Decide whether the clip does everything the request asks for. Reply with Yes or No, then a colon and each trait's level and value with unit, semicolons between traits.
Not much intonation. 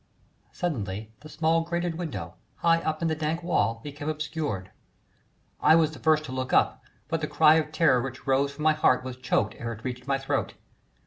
No: average, 3.8 semitones